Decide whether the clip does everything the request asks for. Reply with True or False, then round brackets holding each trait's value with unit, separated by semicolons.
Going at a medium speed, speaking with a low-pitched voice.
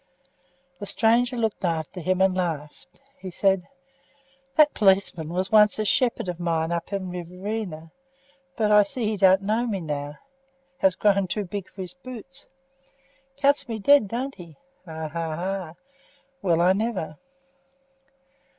False (150 wpm; 190 Hz)